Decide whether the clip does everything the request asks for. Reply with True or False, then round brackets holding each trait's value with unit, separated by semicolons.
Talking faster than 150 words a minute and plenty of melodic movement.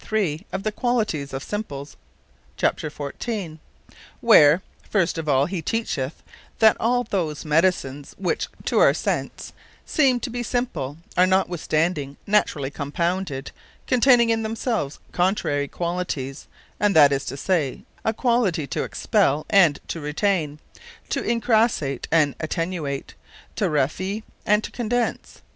False (135 wpm; 6.9 semitones)